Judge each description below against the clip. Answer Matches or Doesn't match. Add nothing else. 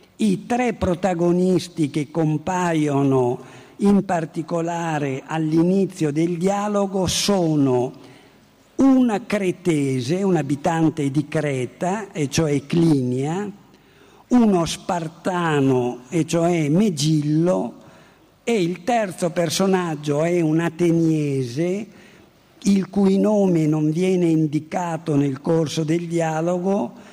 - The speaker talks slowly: Matches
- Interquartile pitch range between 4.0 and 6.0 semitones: Doesn't match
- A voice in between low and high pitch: Matches